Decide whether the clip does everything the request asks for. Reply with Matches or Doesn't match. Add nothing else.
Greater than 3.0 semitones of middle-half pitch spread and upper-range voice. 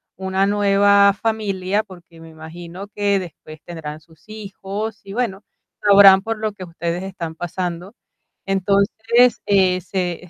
Doesn't match